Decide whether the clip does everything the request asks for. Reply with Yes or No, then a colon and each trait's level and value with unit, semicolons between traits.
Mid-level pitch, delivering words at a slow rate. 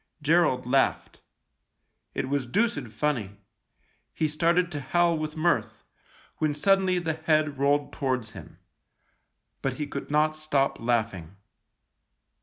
Yes: medium, 145 Hz; slow, 120 wpm